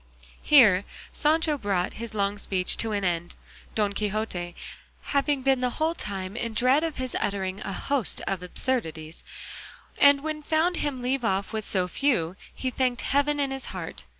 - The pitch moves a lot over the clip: Yes, wide, 6.4 semitones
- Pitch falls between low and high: No, high, 230 Hz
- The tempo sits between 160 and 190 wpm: Yes, average, 175 wpm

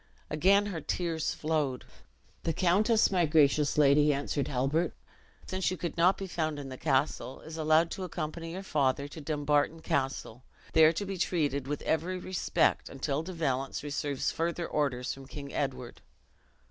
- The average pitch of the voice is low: No, medium, 155 Hz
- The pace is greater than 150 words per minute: Yes, average, 165 wpm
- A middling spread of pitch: Yes, average, 3.4 semitones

